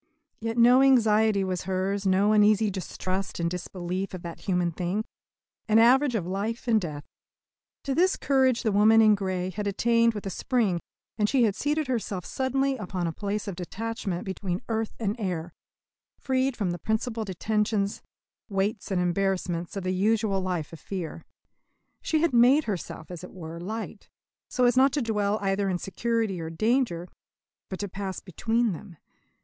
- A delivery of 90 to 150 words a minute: No, average, 170 wpm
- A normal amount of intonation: Yes, average, 3.7 semitones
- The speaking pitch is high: Yes, high, 205 Hz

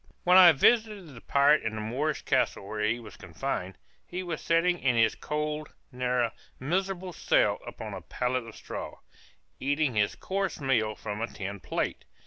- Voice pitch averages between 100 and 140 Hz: Yes, low, 135 Hz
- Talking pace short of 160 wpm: No, average, 175 wpm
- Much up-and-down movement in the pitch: Yes, wide, 7.0 semitones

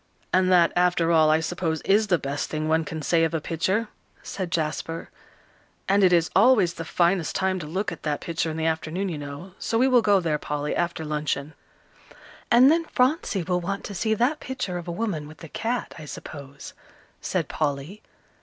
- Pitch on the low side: No, medium, 170 Hz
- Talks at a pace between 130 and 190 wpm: No, average, 200 wpm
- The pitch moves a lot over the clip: No, average, 3.9 semitones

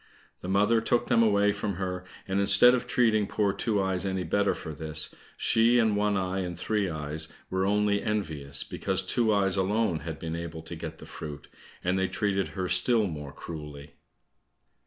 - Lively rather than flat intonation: No, average, 3.9 semitones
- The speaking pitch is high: No, very low, 95 Hz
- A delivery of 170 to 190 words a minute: Yes, average, 185 wpm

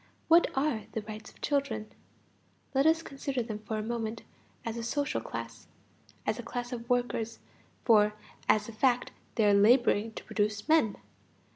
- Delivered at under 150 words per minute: No, average, 165 wpm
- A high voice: Yes, high, 230 Hz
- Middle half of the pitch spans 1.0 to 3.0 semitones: No, average, 3.4 semitones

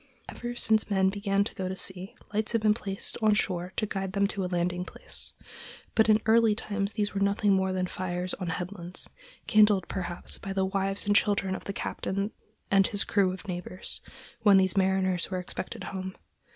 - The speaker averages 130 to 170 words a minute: No, average, 195 wpm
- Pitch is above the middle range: Yes, high, 195 Hz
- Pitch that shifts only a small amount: Yes, narrow, 1.7 semitones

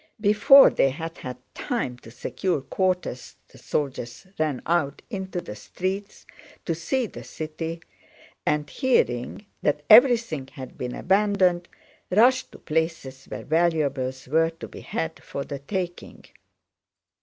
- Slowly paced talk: Yes, slow, 130 wpm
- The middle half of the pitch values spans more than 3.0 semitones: Yes, wide, 5.6 semitones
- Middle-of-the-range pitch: Yes, medium, 165 Hz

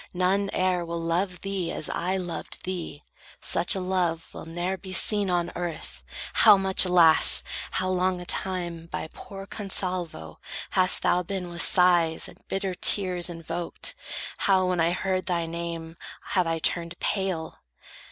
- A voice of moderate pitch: Yes, medium, 180 Hz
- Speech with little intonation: Yes, narrow, 1.9 semitones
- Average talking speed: Yes, average, 155 wpm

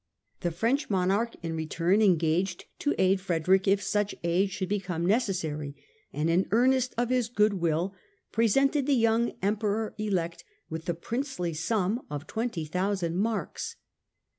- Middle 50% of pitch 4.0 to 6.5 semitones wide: Yes, average, 4.8 semitones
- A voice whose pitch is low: No, high, 195 Hz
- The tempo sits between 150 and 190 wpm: No, average, 140 wpm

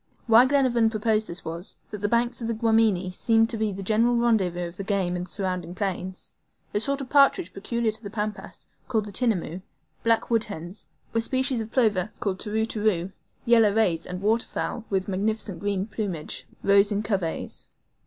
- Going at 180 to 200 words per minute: Yes, average, 185 wpm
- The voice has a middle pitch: No, high, 210 Hz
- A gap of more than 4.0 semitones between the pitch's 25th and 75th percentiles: No, average, 3.3 semitones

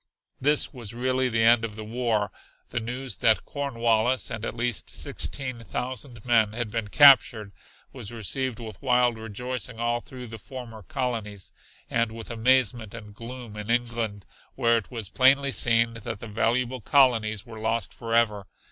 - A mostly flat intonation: Yes, narrow, 2.2 semitones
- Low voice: Yes, low, 115 Hz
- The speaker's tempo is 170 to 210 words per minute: No, average, 160 wpm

